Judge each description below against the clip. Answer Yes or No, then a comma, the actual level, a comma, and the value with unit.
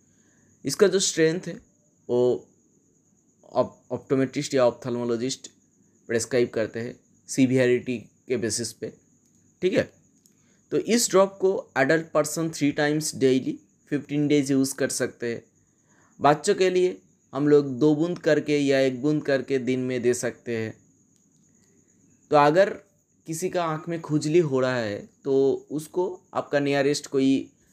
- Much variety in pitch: No, average, 4.1 semitones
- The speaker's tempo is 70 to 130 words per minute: No, fast, 140 wpm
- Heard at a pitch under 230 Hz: Yes, medium, 140 Hz